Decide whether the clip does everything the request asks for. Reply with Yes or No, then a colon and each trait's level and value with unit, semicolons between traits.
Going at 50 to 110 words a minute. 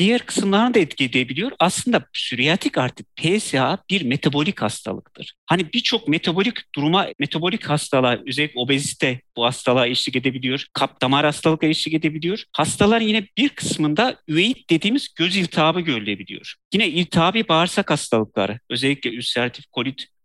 No: average, 135 wpm